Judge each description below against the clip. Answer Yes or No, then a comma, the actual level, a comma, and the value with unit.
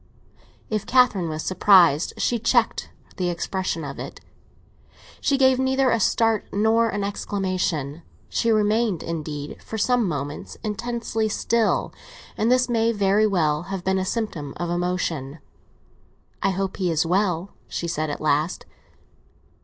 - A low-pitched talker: No, high, 195 Hz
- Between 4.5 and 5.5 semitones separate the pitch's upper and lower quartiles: Yes, average, 5.1 semitones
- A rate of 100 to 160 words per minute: Yes, average, 140 wpm